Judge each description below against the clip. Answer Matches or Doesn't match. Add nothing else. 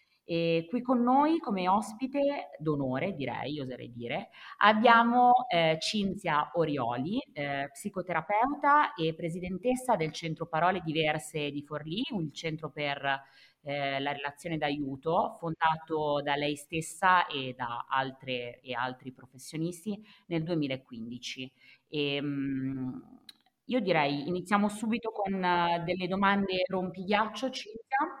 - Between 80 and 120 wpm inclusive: Matches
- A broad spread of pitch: Matches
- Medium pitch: Matches